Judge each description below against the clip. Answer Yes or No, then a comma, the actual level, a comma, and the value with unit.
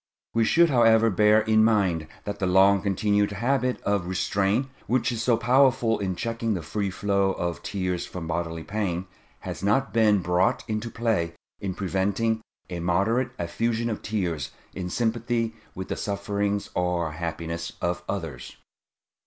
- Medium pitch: No, low, 100 Hz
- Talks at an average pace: Yes, average, 155 wpm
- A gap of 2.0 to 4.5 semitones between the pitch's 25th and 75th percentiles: Yes, average, 4.1 semitones